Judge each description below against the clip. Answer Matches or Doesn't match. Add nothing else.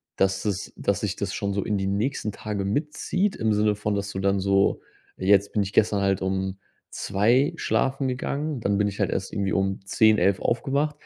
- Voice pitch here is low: Matches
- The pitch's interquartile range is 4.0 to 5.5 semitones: Doesn't match